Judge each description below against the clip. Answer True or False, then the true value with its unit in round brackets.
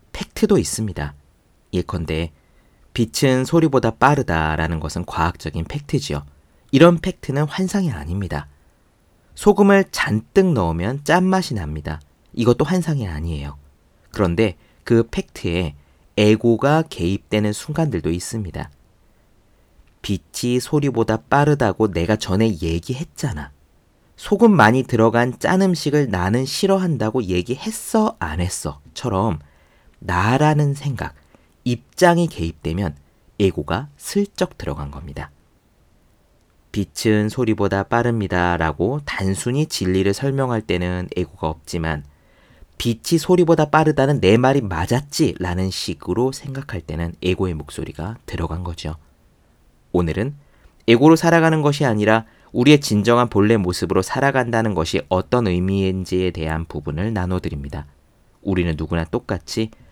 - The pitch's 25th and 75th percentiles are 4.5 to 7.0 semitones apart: False (8.1 semitones)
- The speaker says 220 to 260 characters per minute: False (285 characters per minute)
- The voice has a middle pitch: False (100 Hz)